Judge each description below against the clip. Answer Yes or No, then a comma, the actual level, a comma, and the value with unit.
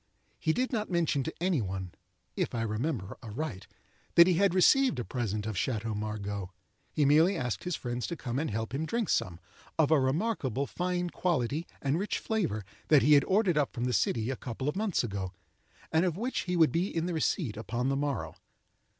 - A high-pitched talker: No, medium, 140 Hz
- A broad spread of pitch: Yes, wide, 7.4 semitones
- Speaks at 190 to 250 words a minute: Yes, average, 200 wpm